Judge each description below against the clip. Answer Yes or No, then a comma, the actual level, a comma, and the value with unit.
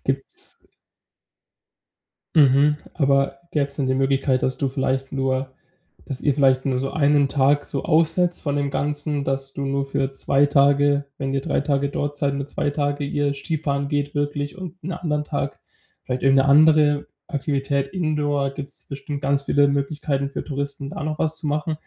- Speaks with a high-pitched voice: No, medium, 140 Hz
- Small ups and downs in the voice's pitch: Yes, narrow, 1.2 semitones